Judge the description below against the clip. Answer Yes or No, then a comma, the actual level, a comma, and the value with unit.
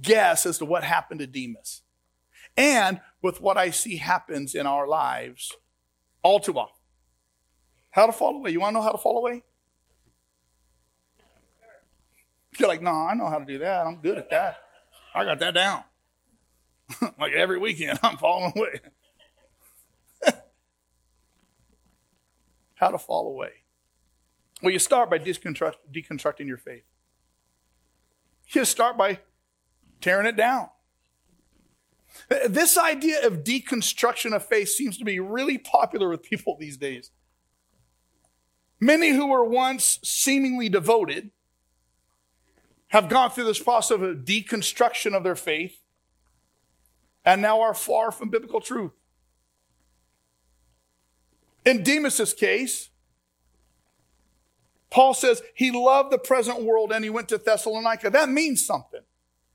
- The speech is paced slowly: Yes, slow, 130 wpm